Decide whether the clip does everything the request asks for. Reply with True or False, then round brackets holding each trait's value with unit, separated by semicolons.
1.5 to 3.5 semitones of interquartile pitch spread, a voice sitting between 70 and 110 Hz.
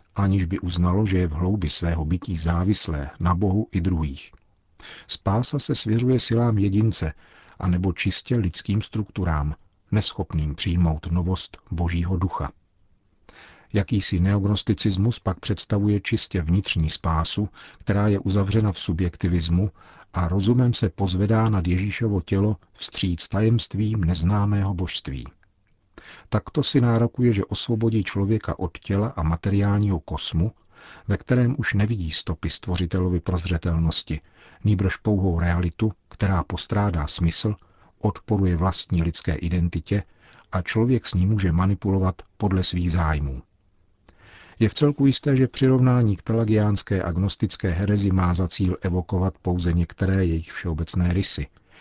True (3.1 semitones; 95 Hz)